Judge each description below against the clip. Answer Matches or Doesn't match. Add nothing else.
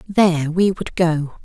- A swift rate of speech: Doesn't match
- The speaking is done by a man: Doesn't match